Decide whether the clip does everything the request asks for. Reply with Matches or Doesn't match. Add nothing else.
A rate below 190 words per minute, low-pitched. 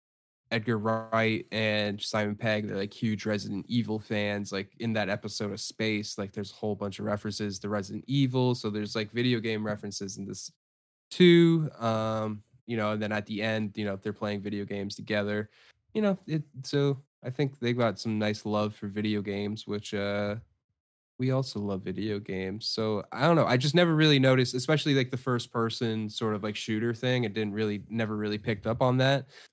Doesn't match